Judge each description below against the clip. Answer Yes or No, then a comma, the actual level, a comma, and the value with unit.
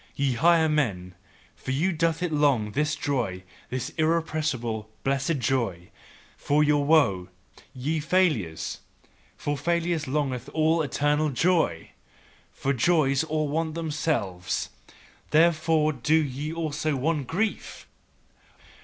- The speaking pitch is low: No, medium, 150 Hz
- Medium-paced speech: No, slow, 115 wpm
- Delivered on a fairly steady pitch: No, average, 3.7 semitones